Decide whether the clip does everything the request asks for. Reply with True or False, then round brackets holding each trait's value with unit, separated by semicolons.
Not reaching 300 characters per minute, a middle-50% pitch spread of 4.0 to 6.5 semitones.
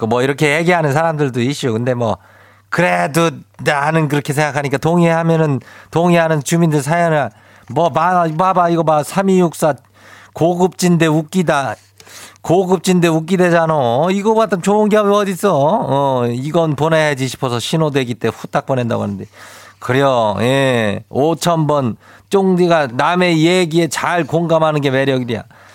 True (290 characters per minute; 5.3 semitones)